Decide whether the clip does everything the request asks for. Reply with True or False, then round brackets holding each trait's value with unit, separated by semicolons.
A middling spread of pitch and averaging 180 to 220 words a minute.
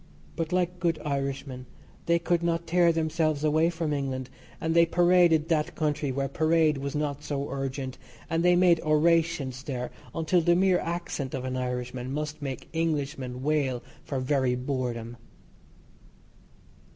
False (3.8 semitones; 150 wpm)